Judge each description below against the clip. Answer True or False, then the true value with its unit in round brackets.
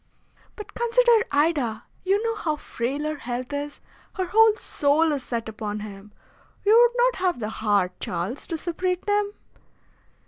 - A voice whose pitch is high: True (310 Hz)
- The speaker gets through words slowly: False (160 wpm)